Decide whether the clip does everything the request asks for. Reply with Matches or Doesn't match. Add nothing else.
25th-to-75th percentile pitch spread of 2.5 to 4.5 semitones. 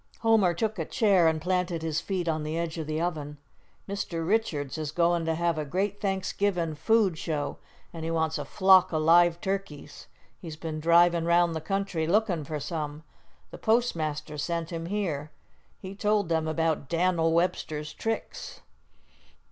Matches